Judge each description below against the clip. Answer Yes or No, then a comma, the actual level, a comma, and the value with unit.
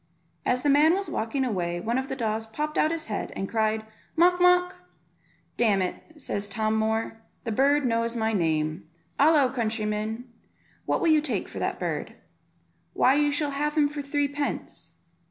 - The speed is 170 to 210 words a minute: Yes, average, 175 wpm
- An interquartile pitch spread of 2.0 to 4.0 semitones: No, average, 5.3 semitones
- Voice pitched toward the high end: Yes, very high, 250 Hz